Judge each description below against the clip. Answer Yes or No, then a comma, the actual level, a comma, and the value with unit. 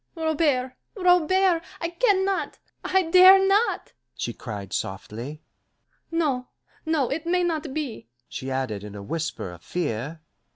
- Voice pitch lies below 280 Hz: No, very high, 300 Hz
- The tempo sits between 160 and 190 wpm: No, slow, 135 wpm